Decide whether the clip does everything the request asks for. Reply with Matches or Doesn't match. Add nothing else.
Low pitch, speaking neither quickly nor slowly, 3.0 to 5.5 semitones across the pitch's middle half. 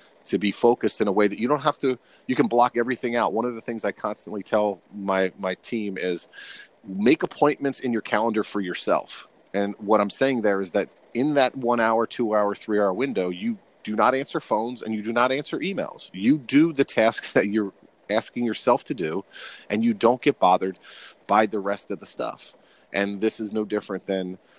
Doesn't match